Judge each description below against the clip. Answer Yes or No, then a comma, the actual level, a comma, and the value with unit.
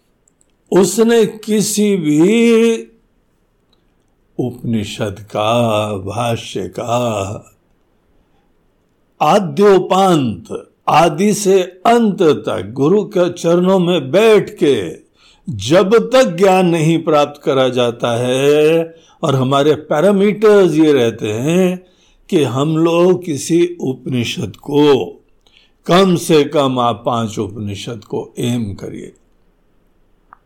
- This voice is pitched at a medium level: Yes, medium, 155 Hz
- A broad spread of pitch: Yes, wide, 8.0 semitones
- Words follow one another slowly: Yes, slow, 95 wpm